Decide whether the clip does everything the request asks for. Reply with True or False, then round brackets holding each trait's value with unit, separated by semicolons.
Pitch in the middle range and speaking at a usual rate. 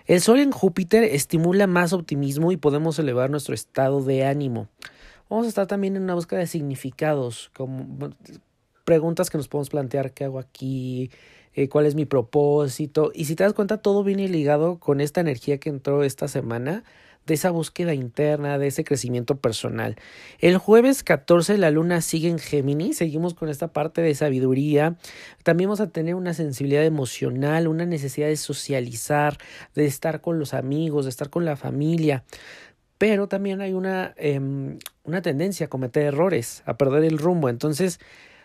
True (155 Hz; 170 wpm)